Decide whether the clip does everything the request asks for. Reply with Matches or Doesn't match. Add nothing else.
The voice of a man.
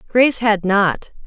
Doesn't match